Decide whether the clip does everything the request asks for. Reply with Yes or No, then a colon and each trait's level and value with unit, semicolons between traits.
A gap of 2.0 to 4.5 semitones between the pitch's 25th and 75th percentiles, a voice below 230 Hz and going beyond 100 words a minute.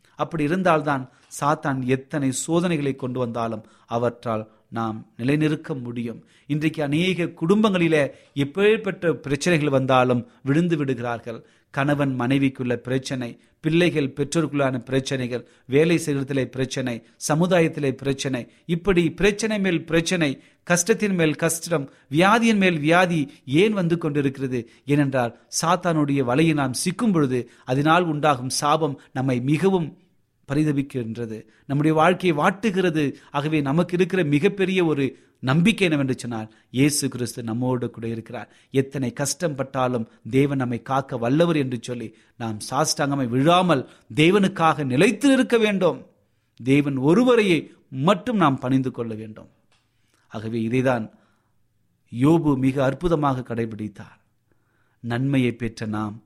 No: average, 5.0 semitones; medium, 140 Hz; average, 110 wpm